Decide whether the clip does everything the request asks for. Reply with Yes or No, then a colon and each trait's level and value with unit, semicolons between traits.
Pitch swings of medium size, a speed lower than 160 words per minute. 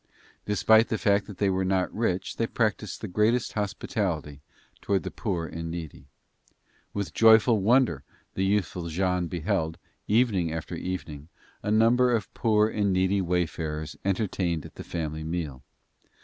Yes: average, 4.3 semitones; average, 150 wpm